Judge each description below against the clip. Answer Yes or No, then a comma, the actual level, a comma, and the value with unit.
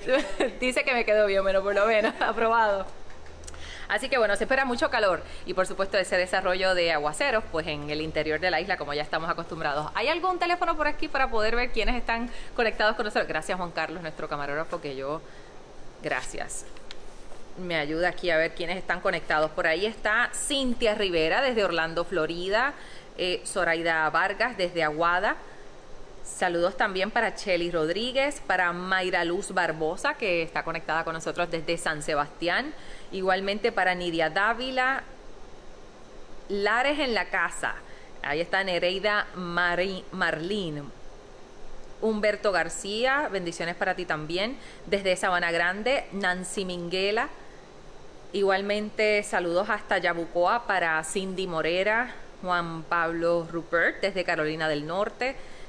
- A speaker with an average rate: Yes, average, 140 wpm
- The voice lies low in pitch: No, medium, 185 Hz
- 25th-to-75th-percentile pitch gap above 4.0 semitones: Yes, average, 4.4 semitones